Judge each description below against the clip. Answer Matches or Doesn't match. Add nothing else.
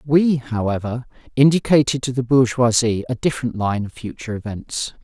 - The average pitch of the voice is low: Matches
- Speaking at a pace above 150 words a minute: Doesn't match